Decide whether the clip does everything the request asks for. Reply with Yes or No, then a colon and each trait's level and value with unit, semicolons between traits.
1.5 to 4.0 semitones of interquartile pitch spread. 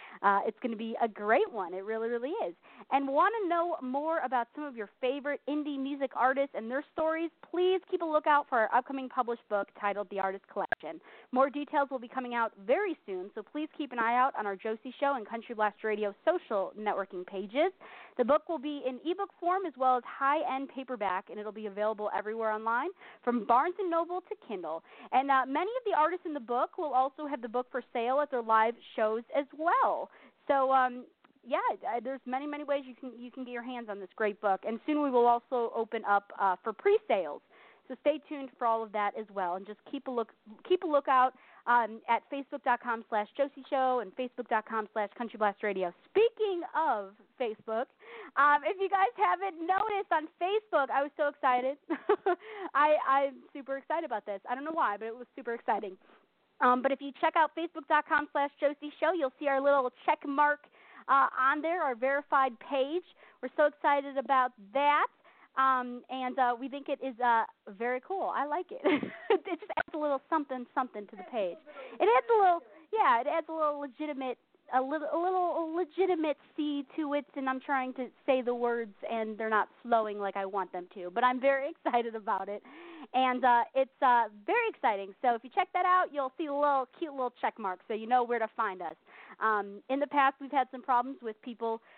No: average, 4.7 semitones